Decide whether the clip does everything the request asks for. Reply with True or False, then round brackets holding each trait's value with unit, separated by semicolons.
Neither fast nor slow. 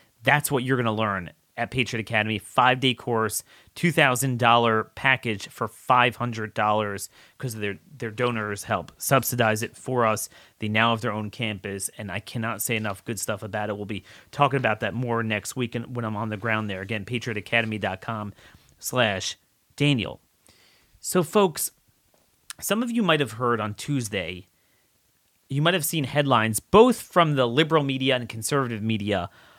True (170 wpm)